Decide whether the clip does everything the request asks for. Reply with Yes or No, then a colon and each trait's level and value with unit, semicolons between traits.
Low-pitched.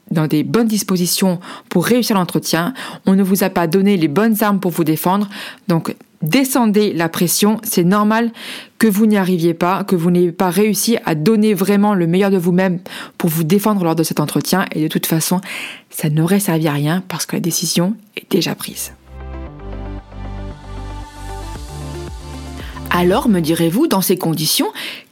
No: medium, 180 Hz